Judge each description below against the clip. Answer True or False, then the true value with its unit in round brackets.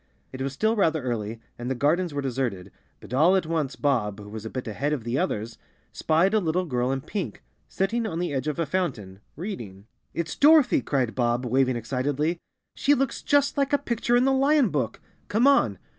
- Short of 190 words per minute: False (205 wpm)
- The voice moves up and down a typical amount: False (8.0 semitones)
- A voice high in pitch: False (145 Hz)